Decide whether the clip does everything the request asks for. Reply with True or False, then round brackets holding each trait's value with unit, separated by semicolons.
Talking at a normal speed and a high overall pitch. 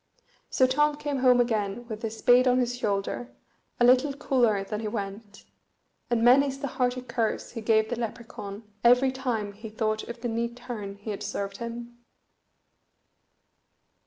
True (160 wpm; 235 Hz)